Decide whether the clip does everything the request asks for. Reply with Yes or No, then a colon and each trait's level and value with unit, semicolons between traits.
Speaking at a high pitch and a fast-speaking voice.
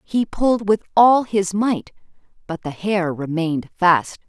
No: high, 195 Hz; average, 155 wpm